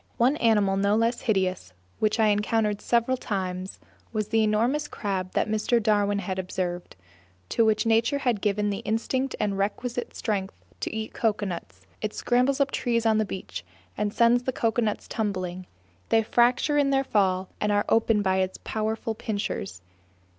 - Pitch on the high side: Yes, high, 215 Hz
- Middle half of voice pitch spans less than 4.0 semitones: Yes, average, 2.9 semitones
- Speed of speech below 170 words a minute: Yes, average, 160 wpm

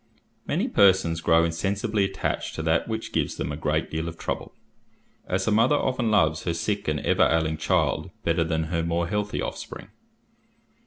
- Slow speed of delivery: No, average, 175 wpm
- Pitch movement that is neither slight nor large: Yes, average, 4.0 semitones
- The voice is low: Yes, very low, 85 Hz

